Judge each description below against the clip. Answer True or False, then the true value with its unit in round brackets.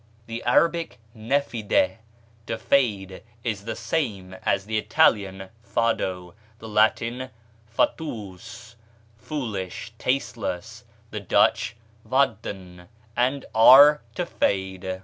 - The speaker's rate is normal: False (95 wpm)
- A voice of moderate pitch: False (110 Hz)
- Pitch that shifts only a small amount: False (4.5 semitones)